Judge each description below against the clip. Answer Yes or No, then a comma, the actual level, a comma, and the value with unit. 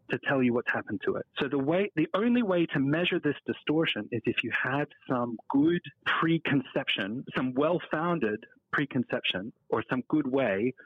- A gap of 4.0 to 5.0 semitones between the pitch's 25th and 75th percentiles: Yes, average, 4.7 semitones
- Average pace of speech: Yes, average, 170 wpm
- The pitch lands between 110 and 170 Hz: Yes, medium, 140 Hz